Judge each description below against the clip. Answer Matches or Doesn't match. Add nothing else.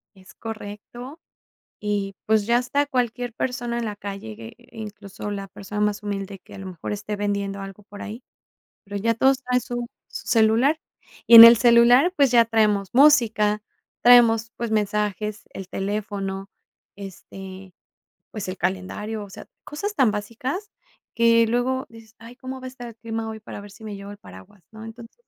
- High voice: Matches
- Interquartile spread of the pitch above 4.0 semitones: Doesn't match